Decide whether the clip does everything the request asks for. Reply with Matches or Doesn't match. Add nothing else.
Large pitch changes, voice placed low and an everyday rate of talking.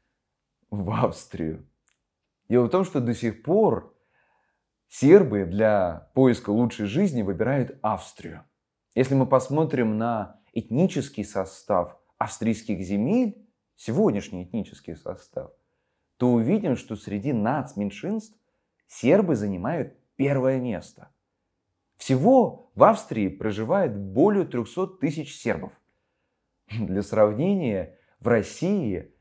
Doesn't match